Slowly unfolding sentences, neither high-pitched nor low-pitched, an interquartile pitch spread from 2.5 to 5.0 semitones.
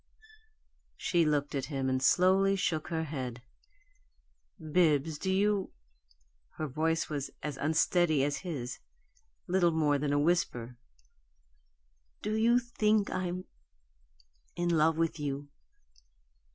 Yes: slow, 120 wpm; medium, 160 Hz; average, 4.1 semitones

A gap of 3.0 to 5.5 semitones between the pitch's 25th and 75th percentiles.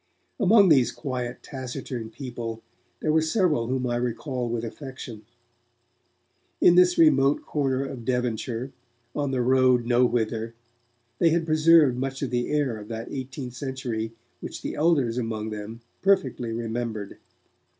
Yes: average, 3.5 semitones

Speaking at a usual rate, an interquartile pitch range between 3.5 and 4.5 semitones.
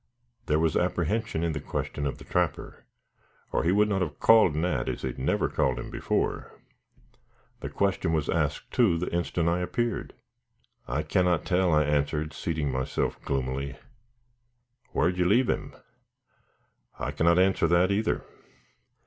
Yes: average, 155 wpm; average, 3.8 semitones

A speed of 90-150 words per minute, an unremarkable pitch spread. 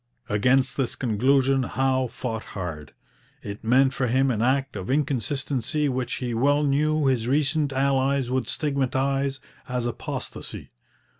No: slow, 135 wpm; narrow, 2.1 semitones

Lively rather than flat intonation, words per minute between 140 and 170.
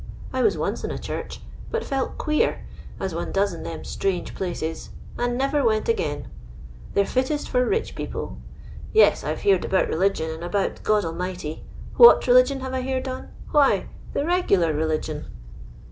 Yes: wide, 8.0 semitones; average, 165 wpm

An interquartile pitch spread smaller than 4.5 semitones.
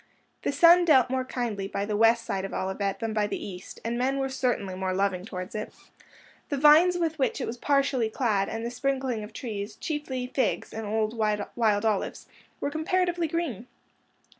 No: average, 4.9 semitones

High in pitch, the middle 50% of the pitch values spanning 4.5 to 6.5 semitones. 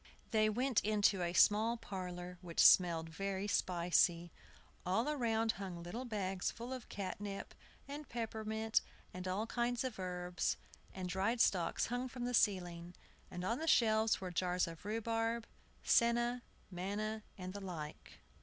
No: high, 205 Hz; average, 4.1 semitones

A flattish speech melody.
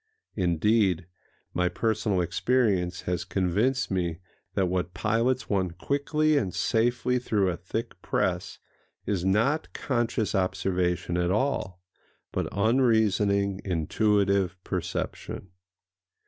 No: average, 4.2 semitones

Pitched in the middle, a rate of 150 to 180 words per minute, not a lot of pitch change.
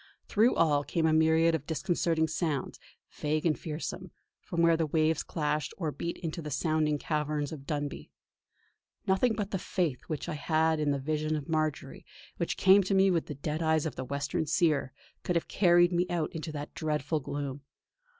No: medium, 155 Hz; average, 190 wpm; narrow, 2.1 semitones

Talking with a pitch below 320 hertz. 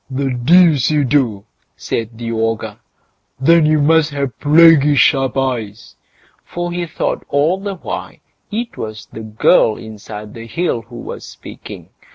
Yes: low, 135 Hz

